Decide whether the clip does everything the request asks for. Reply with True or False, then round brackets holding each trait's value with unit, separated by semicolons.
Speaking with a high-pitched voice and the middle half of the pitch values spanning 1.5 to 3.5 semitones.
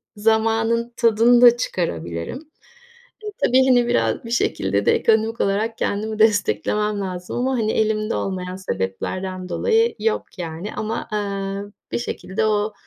True (215 Hz; 3.1 semitones)